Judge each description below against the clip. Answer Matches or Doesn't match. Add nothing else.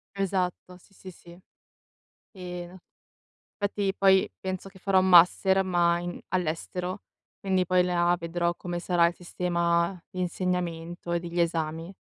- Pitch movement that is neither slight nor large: Doesn't match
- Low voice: Doesn't match